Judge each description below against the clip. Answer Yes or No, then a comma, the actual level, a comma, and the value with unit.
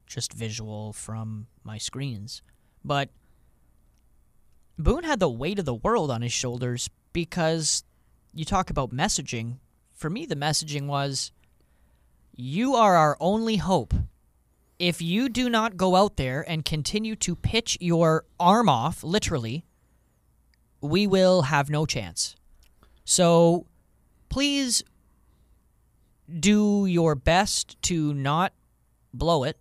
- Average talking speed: No, slow, 120 wpm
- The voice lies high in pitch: No, medium, 145 Hz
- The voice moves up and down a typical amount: No, wide, 8.5 semitones